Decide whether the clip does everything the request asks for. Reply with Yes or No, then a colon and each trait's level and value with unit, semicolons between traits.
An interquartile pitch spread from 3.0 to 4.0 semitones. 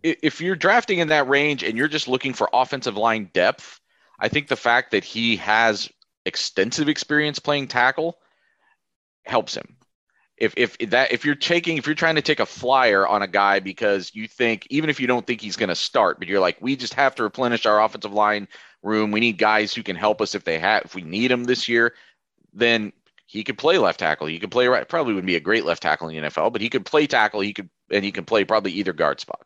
No: wide, 5.6 semitones